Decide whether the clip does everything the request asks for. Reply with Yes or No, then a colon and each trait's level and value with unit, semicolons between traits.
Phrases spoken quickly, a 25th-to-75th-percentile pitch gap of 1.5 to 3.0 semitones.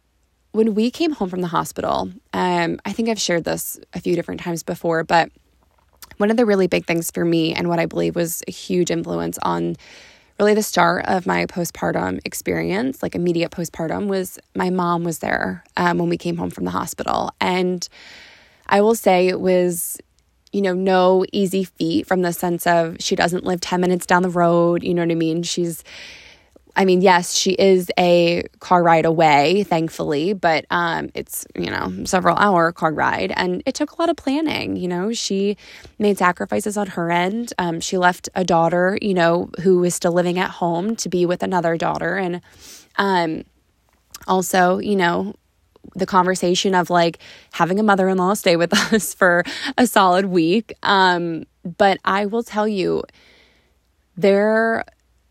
No: average, 180 wpm; narrow, 2.4 semitones